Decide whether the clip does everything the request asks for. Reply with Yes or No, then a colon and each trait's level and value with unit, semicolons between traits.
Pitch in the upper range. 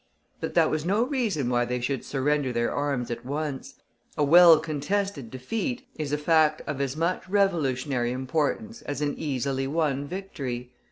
No: medium, 145 Hz